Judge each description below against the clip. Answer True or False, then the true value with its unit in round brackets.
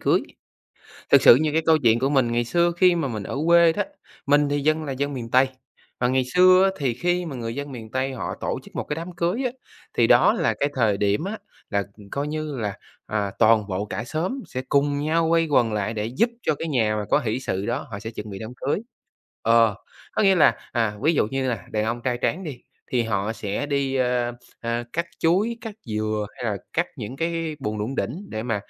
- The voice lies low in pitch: True (130 Hz)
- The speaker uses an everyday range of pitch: False (6.0 semitones)